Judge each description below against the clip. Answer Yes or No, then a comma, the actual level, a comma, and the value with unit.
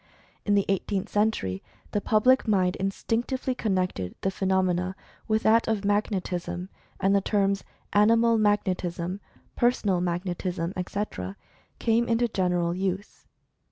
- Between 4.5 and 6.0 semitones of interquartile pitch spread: No, average, 3.1 semitones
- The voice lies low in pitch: No, high, 195 Hz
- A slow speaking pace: Yes, slow, 125 wpm